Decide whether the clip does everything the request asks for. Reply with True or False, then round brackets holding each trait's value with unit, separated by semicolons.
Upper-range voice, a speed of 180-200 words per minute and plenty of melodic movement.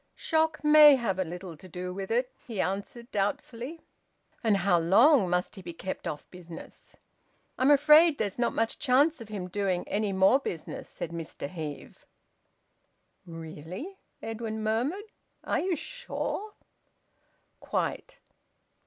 False (215 Hz; 140 wpm; 7.5 semitones)